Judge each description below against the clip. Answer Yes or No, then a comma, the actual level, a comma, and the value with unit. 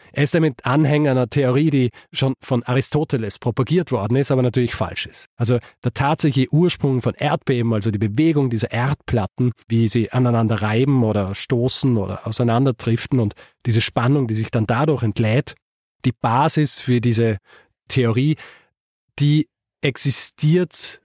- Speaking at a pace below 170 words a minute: Yes, average, 145 wpm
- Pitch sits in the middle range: No, low, 125 Hz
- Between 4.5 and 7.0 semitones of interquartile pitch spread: No, average, 3.6 semitones